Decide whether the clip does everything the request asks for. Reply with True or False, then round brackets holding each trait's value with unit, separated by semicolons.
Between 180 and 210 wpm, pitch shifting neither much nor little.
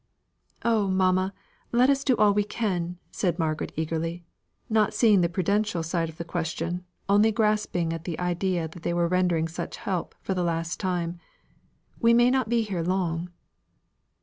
False (170 wpm; 3.7 semitones)